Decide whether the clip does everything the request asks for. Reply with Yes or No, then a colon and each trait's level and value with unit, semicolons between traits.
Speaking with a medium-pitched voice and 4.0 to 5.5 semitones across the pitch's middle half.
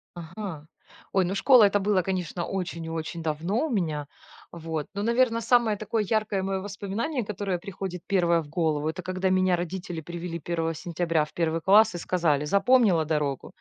No: medium, 180 Hz; average, 3.5 semitones